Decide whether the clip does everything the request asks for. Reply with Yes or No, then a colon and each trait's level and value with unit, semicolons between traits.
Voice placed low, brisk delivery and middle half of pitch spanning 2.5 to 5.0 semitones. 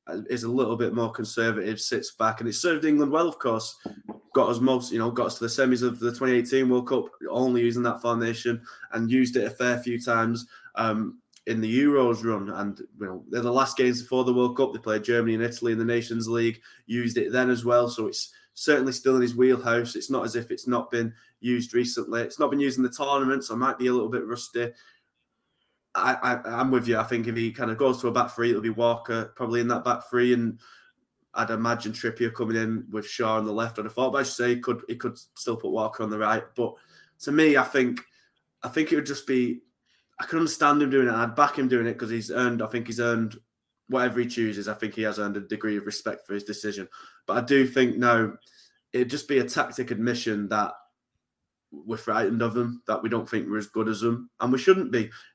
No: low, 120 Hz; fast, 245 wpm; narrow, 1.9 semitones